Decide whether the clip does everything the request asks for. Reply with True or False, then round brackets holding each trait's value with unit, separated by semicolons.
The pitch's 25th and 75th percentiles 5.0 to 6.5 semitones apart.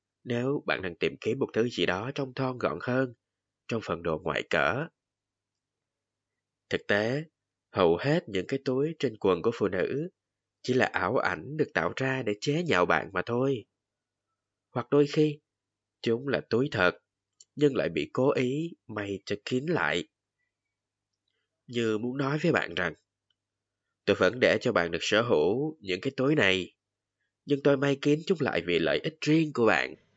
True (5.6 semitones)